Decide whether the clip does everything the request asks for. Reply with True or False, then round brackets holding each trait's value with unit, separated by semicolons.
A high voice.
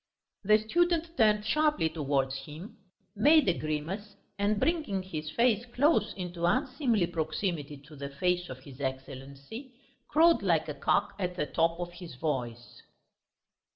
False (175 Hz)